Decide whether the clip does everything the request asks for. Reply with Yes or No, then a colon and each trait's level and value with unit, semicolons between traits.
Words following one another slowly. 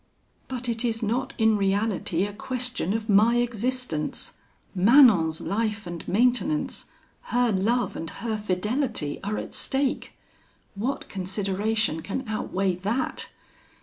Yes: slow, 120 wpm